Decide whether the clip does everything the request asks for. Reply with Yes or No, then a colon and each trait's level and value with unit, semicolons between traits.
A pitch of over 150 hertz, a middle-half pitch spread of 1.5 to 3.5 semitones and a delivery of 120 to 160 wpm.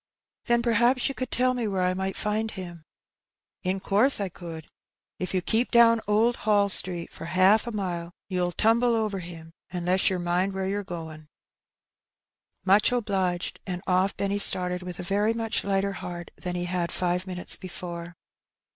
No: high, 190 Hz; average, 3.2 semitones; average, 185 wpm